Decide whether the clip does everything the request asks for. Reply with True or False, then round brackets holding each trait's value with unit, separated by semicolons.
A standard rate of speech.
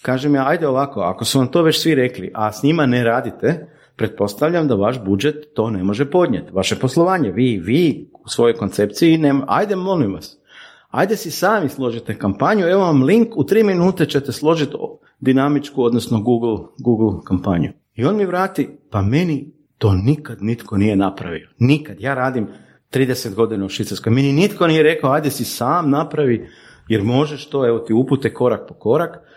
False (180 wpm)